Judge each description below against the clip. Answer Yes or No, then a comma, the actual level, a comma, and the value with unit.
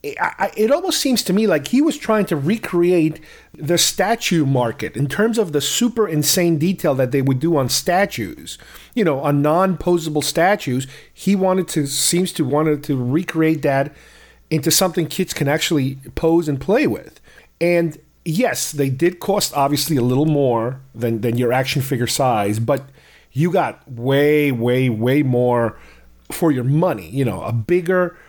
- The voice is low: No, medium, 150 Hz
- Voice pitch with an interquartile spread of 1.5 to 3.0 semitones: No, average, 4.8 semitones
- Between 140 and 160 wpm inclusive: No, average, 170 wpm